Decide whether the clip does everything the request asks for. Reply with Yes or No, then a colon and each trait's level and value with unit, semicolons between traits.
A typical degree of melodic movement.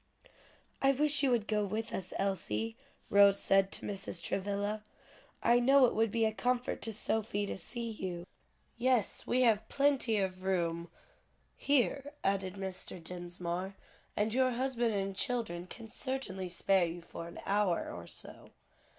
Yes: average, 4.2 semitones